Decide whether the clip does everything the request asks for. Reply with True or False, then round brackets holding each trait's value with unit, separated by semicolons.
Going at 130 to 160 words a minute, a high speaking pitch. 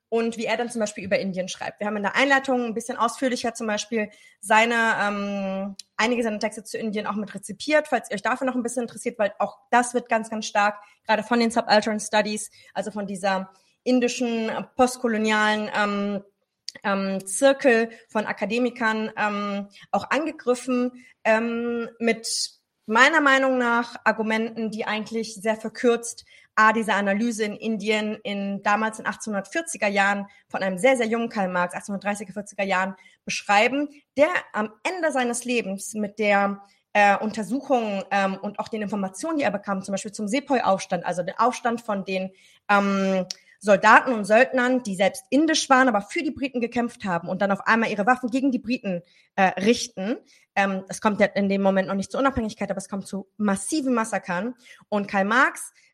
False (180 wpm; 215 Hz)